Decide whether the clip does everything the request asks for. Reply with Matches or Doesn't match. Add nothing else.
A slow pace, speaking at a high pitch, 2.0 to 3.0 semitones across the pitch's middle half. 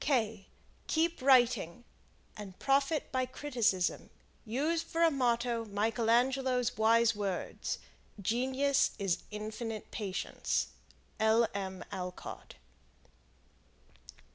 Doesn't match